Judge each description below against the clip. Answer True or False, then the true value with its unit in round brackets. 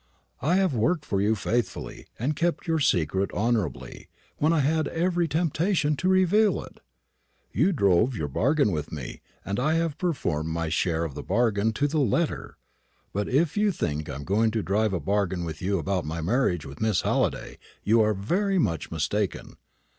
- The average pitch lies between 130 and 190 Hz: False (110 Hz)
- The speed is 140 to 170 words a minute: False (185 wpm)